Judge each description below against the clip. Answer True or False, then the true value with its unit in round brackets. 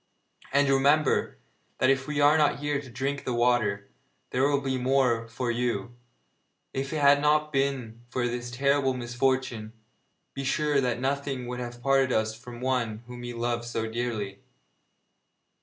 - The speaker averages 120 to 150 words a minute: False (165 wpm)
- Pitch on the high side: False (125 Hz)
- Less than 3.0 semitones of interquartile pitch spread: True (2.5 semitones)